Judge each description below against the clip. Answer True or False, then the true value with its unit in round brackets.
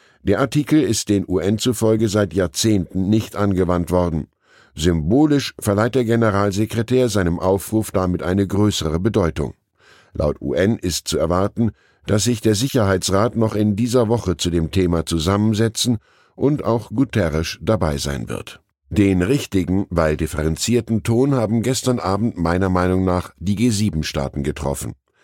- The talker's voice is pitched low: True (100 Hz)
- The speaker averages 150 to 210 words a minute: False (140 wpm)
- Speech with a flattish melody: False (4.3 semitones)